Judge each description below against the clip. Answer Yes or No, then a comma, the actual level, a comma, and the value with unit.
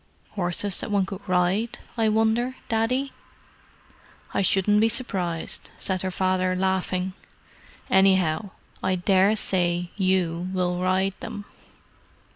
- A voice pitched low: No, high, 190 Hz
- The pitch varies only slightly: Yes, narrow, 2.3 semitones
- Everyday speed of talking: No, slow, 110 wpm